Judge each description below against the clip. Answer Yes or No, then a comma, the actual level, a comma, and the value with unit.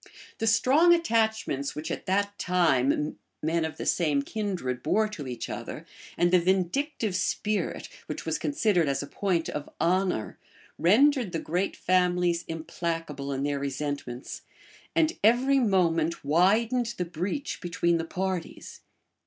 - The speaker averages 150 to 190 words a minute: No, average, 140 wpm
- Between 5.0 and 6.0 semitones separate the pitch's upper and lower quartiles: Yes, wide, 5.4 semitones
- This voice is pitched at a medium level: Yes, medium, 180 Hz